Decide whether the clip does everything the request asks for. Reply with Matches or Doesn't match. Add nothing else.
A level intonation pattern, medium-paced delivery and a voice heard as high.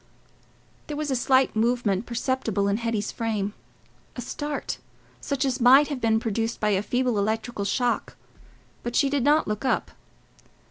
Doesn't match